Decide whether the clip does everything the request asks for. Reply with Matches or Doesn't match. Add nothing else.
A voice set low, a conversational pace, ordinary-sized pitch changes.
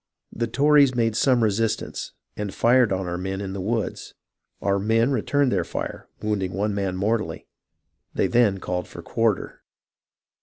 Matches